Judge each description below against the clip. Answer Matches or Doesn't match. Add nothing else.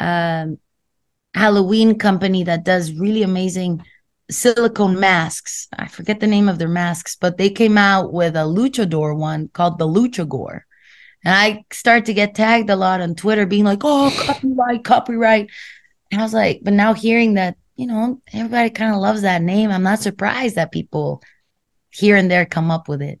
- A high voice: Matches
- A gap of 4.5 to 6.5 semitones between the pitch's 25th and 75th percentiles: Doesn't match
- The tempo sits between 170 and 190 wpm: Matches